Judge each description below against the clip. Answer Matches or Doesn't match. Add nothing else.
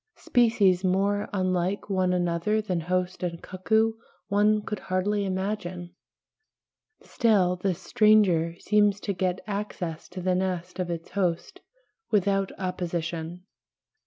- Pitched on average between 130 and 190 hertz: Matches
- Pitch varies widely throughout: Doesn't match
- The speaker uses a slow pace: Matches